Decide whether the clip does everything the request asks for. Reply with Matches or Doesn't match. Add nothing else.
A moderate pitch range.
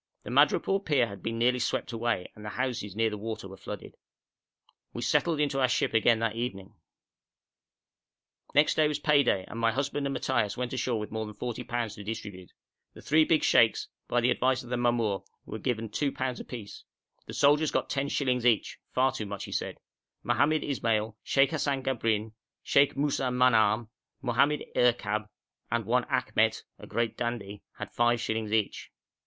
Matches